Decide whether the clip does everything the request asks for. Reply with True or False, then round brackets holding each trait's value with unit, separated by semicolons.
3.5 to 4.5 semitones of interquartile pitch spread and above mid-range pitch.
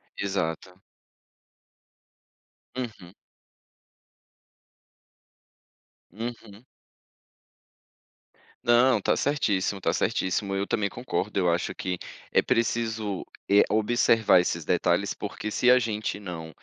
False (3.8 semitones; 100 Hz)